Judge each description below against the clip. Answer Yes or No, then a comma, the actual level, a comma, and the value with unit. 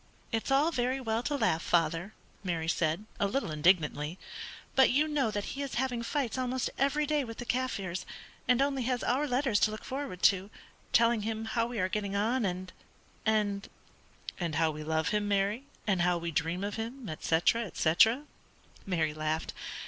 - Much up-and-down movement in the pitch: Yes, wide, 6.3 semitones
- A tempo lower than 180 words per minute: No, average, 185 wpm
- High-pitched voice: Yes, high, 215 Hz